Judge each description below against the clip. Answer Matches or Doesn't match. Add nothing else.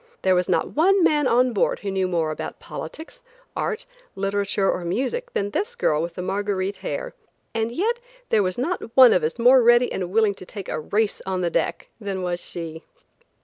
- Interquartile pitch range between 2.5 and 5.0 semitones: Doesn't match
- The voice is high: Matches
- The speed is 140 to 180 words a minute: Doesn't match